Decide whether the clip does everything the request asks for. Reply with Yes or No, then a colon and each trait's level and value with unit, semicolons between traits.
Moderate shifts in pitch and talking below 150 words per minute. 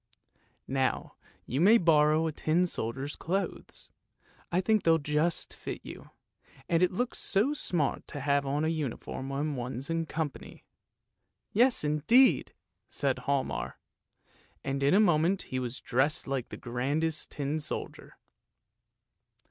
Yes: average, 3.9 semitones; average, 140 wpm